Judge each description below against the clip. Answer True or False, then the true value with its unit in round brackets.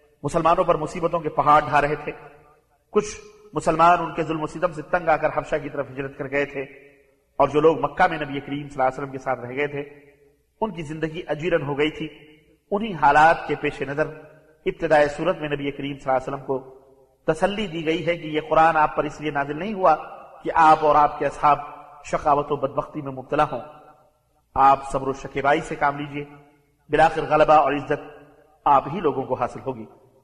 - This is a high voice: False (150 Hz)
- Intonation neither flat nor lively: False (1.8 semitones)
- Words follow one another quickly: True (210 wpm)